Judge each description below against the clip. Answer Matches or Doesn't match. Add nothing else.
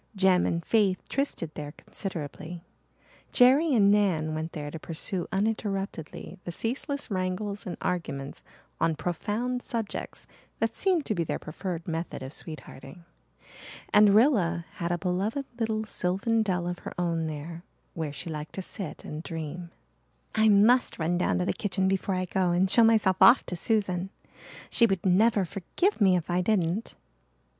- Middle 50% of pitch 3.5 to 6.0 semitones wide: Matches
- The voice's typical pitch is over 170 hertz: Matches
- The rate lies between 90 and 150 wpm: Doesn't match